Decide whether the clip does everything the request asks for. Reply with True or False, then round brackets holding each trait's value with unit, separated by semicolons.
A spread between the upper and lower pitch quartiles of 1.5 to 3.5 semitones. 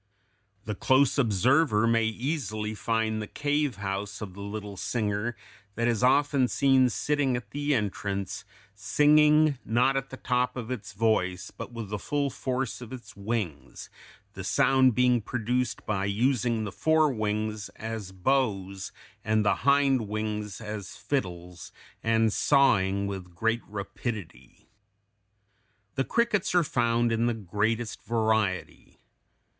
False (4.1 semitones)